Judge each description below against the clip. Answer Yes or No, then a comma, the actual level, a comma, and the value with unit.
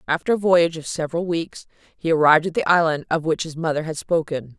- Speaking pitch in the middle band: Yes, medium, 160 Hz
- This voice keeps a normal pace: No, fast, 220 wpm